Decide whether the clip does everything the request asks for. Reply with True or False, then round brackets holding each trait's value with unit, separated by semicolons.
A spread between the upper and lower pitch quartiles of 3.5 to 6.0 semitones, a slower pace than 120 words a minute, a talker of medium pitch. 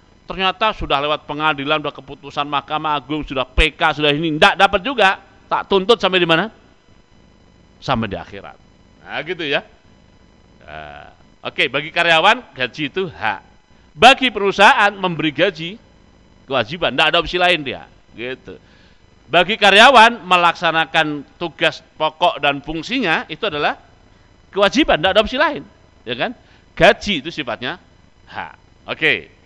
False (5.4 semitones; 130 wpm; 160 Hz)